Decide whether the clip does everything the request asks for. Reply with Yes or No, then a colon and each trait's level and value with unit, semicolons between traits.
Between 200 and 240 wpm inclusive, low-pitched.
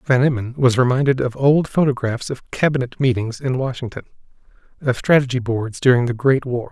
No: average, 170 wpm; low, 130 Hz